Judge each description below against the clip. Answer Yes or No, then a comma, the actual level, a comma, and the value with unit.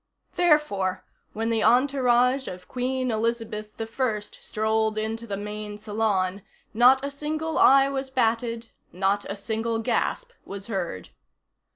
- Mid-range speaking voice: No, high, 225 Hz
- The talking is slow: Yes, slow, 130 wpm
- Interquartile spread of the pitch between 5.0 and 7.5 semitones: No, average, 3.6 semitones